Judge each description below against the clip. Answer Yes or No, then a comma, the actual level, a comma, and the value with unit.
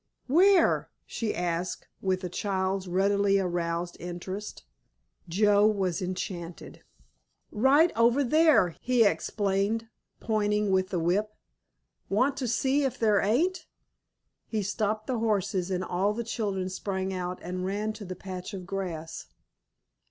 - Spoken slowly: Yes, slow, 130 wpm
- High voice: Yes, high, 200 Hz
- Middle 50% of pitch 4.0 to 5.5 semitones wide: No, average, 3.1 semitones